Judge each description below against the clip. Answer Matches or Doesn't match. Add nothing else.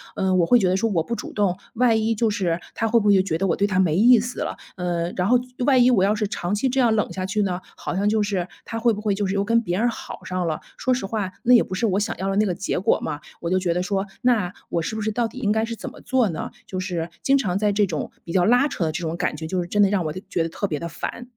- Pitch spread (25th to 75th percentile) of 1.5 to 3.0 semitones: Doesn't match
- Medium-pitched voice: Doesn't match